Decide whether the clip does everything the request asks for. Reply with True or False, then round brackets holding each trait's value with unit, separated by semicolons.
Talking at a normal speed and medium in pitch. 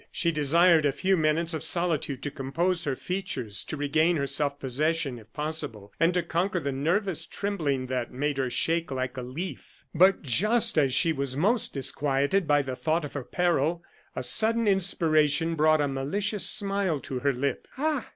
True (180 wpm; 155 Hz)